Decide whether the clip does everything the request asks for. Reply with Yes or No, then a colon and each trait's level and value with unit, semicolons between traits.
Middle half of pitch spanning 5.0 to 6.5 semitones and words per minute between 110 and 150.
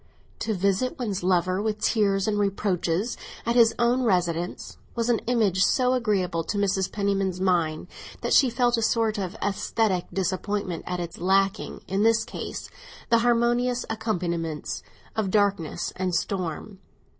No: average, 3.7 semitones; average, 145 wpm